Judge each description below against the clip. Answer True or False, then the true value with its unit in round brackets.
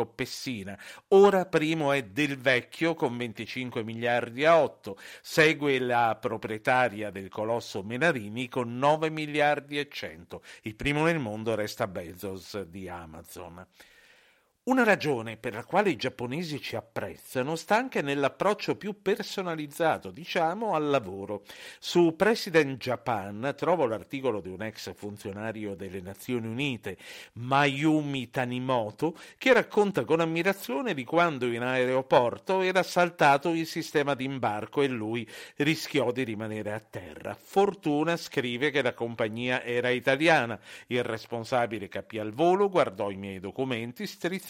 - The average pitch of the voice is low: True (130 Hz)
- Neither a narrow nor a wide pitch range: False (6.2 semitones)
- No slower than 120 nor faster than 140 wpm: True (135 wpm)